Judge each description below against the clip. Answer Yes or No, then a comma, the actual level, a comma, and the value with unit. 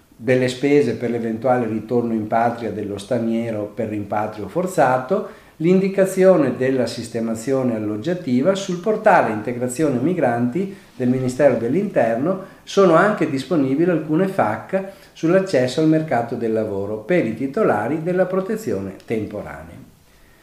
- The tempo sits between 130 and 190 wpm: No, slow, 115 wpm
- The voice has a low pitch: Yes, low, 130 Hz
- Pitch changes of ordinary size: No, wide, 7.7 semitones